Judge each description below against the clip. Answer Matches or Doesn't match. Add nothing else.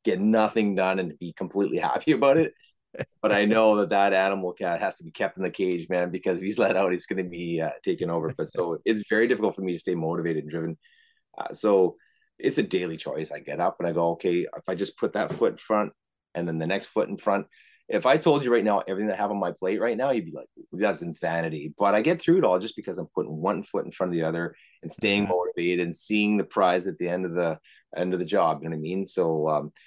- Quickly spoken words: Matches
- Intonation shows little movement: Doesn't match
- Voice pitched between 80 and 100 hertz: Matches